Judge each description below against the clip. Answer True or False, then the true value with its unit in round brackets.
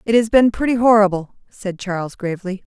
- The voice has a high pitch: True (205 Hz)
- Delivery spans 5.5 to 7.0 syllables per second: True (5.8 syllables/s)